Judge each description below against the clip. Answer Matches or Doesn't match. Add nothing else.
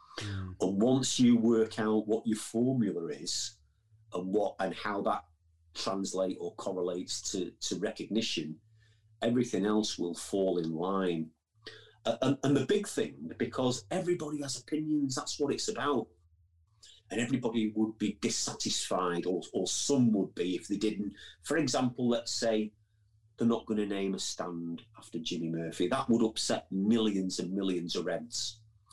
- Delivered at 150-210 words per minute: Matches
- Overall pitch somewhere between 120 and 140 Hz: Doesn't match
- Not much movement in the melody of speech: Doesn't match